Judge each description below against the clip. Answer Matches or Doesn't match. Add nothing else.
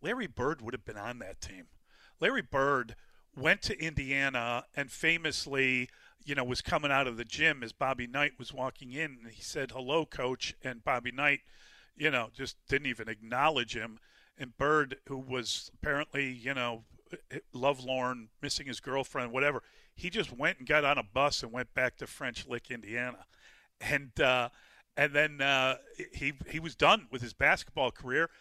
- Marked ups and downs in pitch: Doesn't match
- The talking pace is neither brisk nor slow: Matches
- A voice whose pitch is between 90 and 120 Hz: Doesn't match